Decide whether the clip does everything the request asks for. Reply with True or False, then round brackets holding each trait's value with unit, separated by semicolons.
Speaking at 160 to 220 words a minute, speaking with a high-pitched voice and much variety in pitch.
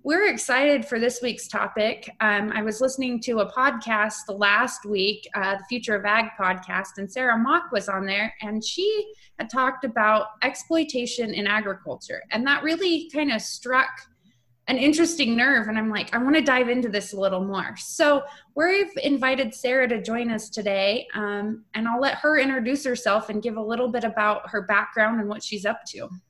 False (190 wpm; 230 Hz; 3.9 semitones)